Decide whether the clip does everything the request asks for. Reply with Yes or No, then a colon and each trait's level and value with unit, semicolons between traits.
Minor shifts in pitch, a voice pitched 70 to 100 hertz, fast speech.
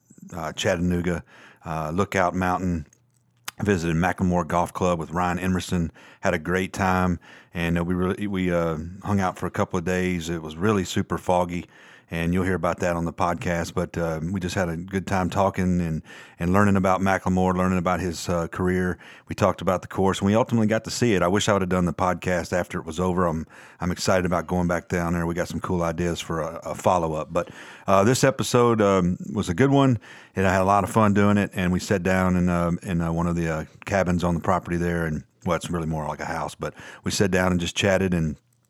Yes: narrow, 2.0 semitones; very low, 90 Hz; fast, 240 wpm